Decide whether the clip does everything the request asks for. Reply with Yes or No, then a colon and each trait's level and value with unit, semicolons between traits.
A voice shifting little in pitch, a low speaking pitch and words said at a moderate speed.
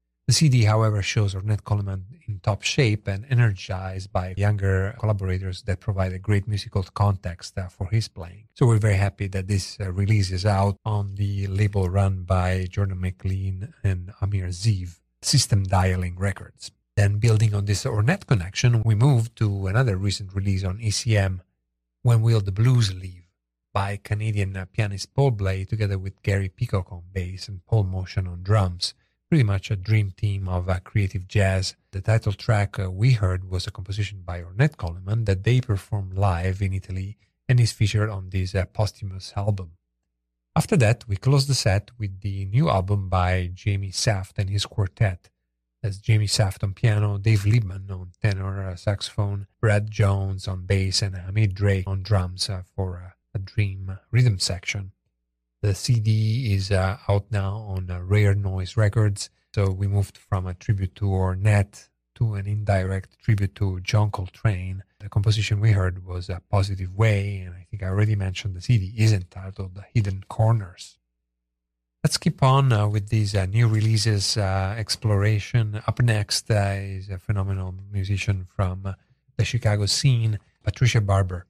Yes: narrow, 2.3 semitones; low, 100 Hz; average, 165 wpm